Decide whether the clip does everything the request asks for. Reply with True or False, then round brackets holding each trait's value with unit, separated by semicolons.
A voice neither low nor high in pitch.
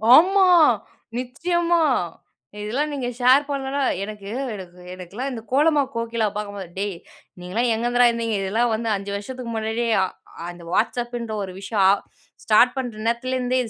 False (235 Hz)